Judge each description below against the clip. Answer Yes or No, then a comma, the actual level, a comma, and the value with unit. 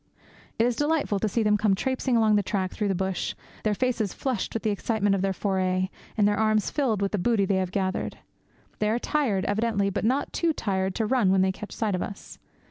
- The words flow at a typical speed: No, fast, 230 wpm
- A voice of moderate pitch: No, high, 210 Hz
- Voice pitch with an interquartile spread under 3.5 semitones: Yes, average, 2.9 semitones